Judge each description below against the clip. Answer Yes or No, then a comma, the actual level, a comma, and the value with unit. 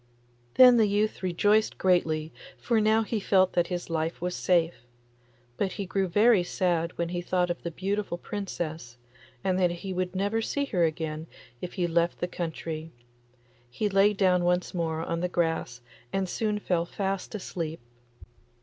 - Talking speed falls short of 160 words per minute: No, average, 165 wpm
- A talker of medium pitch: Yes, medium, 180 Hz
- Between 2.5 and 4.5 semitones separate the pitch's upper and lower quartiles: Yes, average, 2.9 semitones